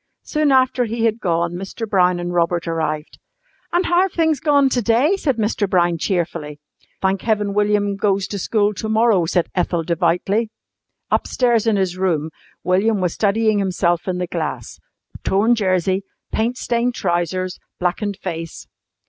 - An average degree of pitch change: Yes, average, 4.4 semitones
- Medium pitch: No, high, 195 Hz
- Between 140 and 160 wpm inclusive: Yes, average, 155 wpm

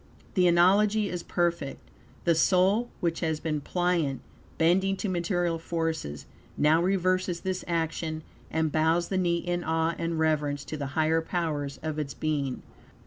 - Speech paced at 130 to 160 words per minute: Yes, average, 150 wpm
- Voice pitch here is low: No, medium, 165 Hz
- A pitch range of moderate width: No, narrow, 2.2 semitones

